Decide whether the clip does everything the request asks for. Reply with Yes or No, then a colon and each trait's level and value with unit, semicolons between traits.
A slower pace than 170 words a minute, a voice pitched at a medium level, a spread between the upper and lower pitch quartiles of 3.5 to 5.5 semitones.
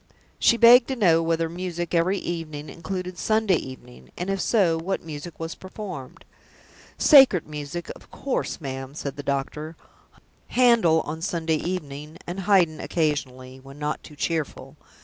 Yes: average, 150 wpm; medium, 165 Hz; average, 4.0 semitones